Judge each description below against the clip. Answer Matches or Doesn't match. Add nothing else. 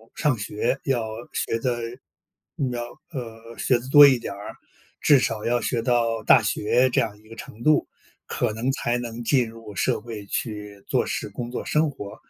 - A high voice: Doesn't match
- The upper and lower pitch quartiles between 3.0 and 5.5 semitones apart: Doesn't match